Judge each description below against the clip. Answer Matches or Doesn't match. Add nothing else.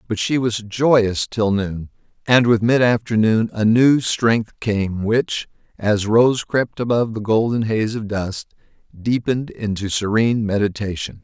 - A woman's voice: Doesn't match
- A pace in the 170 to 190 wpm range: Doesn't match